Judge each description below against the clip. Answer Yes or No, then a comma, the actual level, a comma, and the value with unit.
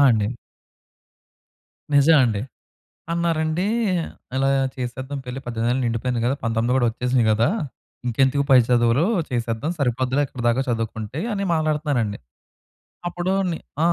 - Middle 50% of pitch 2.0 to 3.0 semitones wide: No, average, 3.8 semitones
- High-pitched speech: No, low, 125 Hz